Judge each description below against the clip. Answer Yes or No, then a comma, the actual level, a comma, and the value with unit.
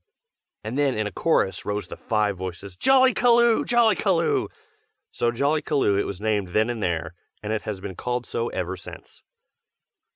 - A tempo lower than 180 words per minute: Yes, average, 160 wpm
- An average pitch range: No, wide, 7.3 semitones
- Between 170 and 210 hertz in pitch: No, low, 110 Hz